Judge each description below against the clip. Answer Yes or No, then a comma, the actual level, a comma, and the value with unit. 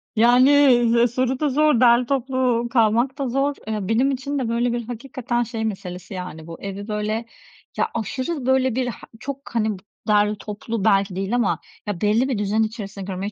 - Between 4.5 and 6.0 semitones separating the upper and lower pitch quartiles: No, average, 3.7 semitones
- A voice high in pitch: Yes, high, 230 Hz